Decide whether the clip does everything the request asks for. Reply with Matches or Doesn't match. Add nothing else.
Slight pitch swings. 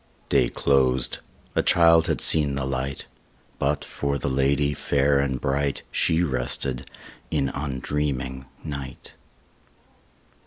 Matches